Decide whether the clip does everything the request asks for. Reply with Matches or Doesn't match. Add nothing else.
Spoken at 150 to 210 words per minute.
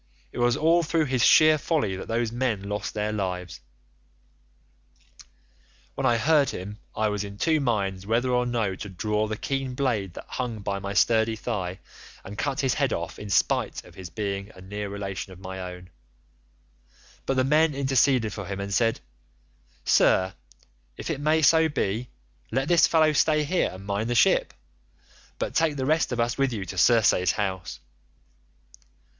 Matches